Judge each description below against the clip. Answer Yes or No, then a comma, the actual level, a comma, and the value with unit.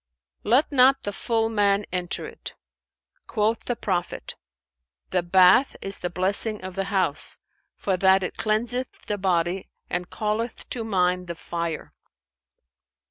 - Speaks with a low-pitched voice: No, high, 195 Hz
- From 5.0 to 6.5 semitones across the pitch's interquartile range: No, average, 3.6 semitones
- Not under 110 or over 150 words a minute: Yes, slow, 135 wpm